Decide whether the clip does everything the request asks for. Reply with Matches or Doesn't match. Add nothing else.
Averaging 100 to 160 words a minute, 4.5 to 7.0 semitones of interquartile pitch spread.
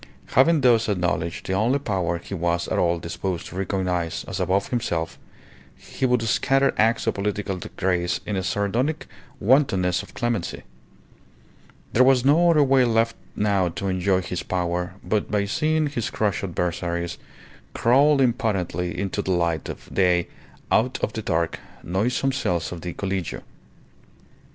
Matches